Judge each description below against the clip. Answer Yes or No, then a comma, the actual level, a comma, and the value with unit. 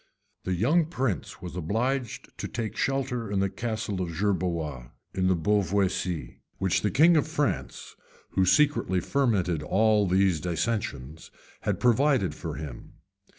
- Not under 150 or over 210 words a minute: No, average, 140 wpm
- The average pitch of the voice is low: Yes, low, 100 Hz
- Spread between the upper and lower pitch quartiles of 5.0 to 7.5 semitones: Yes, wide, 5.5 semitones